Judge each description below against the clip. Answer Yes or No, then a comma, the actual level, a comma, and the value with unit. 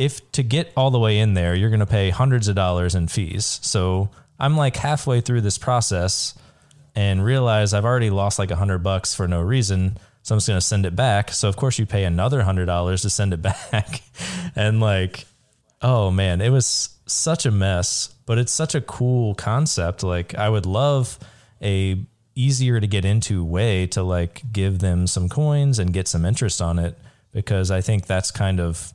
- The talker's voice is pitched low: Yes, low, 105 Hz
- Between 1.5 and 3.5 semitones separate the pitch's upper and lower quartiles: No, average, 4.9 semitones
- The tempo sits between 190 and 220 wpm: Yes, average, 200 wpm